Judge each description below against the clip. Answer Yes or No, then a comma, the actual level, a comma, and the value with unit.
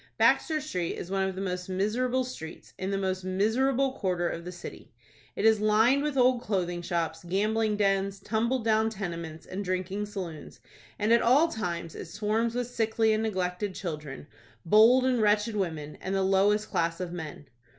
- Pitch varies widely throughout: No, average, 3.7 semitones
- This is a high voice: Yes, high, 200 Hz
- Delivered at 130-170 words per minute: No, average, 180 wpm